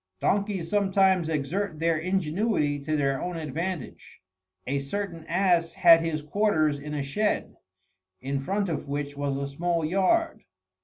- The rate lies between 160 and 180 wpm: No, average, 145 wpm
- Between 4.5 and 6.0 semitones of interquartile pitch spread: Yes, average, 4.8 semitones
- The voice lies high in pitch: No, medium, 165 Hz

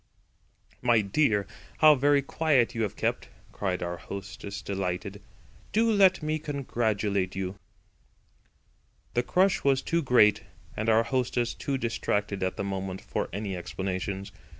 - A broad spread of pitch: Yes, wide, 6.0 semitones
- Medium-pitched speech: No, low, 110 Hz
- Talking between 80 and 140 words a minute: Yes, slow, 135 wpm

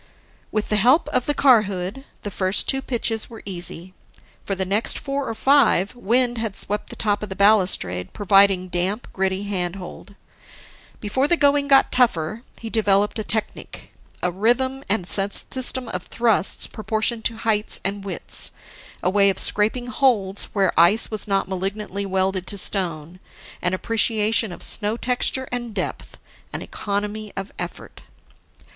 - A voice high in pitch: Yes, high, 210 Hz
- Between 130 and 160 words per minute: Yes, average, 155 wpm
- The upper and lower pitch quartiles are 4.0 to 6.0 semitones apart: No, average, 3.4 semitones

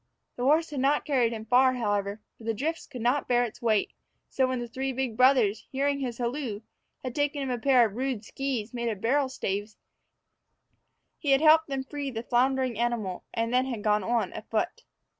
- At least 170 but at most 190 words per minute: No, average, 200 wpm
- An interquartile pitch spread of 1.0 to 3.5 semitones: Yes, average, 3.1 semitones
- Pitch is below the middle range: No, very high, 250 Hz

